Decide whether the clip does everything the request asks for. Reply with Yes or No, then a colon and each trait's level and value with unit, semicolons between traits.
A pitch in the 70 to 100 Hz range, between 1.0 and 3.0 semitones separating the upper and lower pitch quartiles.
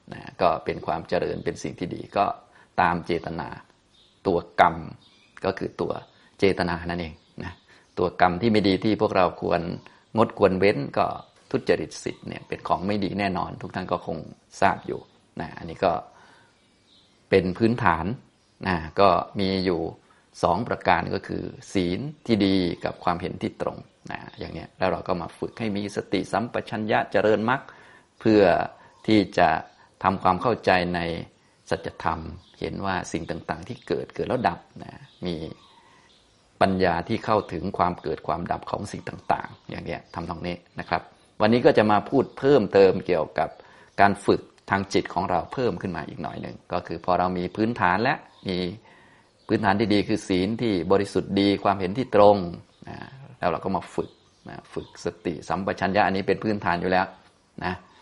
Yes: very low, 95 Hz; narrow, 2.6 semitones